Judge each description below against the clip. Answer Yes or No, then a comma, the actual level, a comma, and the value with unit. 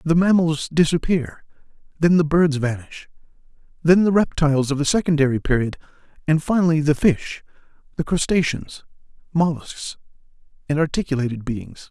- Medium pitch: Yes, medium, 155 Hz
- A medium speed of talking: No, slow, 120 wpm